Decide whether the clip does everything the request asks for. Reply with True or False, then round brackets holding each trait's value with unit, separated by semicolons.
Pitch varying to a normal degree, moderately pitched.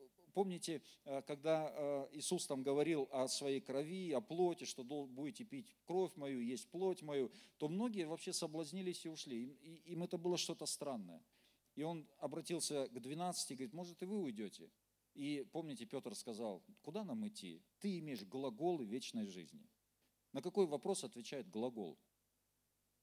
True (4.7 semitones; 165 Hz)